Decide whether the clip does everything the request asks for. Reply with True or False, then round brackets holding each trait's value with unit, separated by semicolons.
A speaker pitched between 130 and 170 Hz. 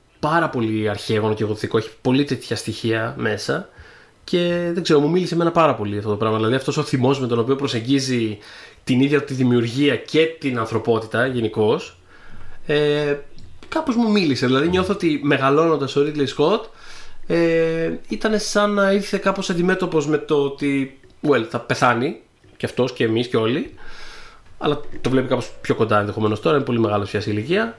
True (135 Hz)